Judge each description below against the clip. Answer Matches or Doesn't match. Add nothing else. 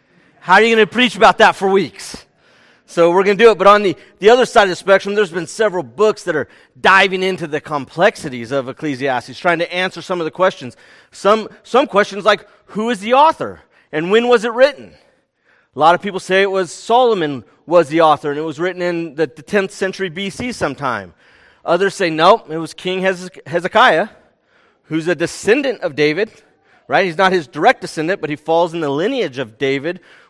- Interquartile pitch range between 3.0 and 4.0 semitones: Doesn't match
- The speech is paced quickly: Matches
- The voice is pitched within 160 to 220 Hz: Matches